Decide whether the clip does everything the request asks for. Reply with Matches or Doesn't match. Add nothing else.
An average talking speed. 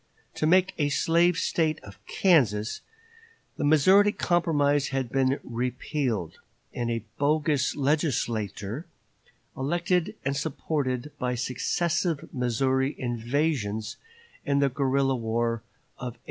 Doesn't match